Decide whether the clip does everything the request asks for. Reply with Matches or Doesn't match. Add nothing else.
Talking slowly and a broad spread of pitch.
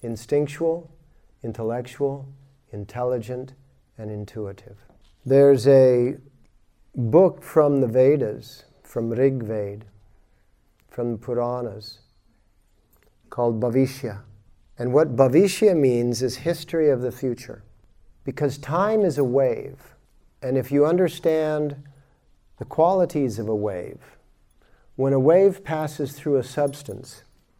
Doesn't match